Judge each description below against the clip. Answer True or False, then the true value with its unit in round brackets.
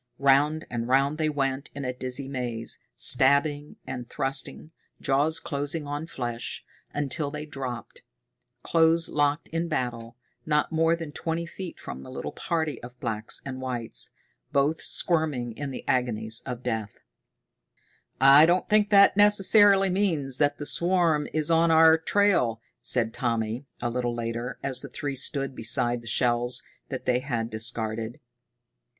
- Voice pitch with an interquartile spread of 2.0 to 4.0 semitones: False (4.7 semitones)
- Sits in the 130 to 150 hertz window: True (140 Hz)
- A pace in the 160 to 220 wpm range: False (150 wpm)